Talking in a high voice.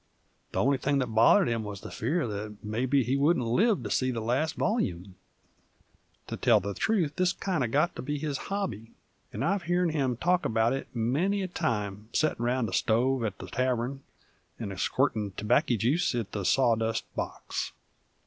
No: low, 125 Hz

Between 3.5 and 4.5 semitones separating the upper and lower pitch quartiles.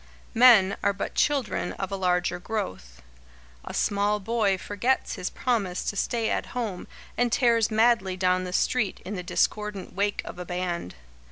Yes: average, 3.8 semitones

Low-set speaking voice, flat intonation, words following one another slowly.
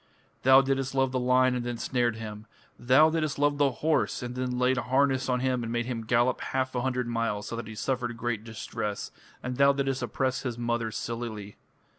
No: low, 125 Hz; narrow, 2.1 semitones; fast, 205 wpm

